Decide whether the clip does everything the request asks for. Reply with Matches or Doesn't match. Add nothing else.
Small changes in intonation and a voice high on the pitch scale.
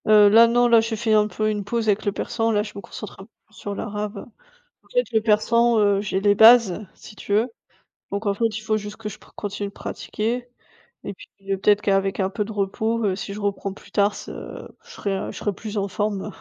Matches